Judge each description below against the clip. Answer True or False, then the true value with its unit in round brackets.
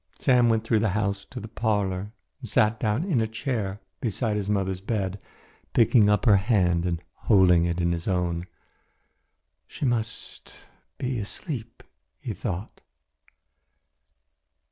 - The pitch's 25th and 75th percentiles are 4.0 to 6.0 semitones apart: False (3.3 semitones)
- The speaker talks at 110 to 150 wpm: True (140 wpm)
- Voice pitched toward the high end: False (105 Hz)